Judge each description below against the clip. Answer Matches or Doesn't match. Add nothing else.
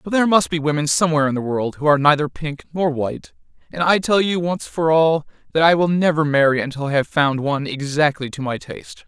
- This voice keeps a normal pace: Doesn't match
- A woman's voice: Doesn't match